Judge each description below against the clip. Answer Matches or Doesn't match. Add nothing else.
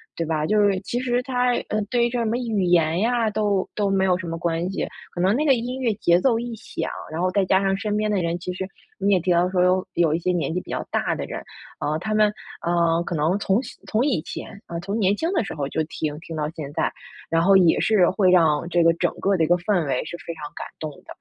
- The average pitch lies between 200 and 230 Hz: Doesn't match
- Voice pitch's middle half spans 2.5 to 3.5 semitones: Doesn't match